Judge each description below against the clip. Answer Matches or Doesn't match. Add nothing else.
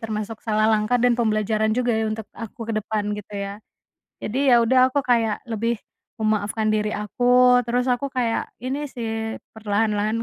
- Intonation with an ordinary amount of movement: Doesn't match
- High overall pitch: Matches